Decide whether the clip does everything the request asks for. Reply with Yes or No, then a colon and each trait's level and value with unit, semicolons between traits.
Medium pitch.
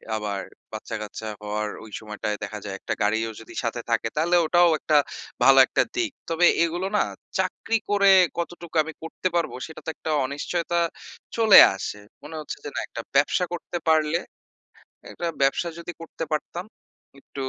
Yes: medium, 155 Hz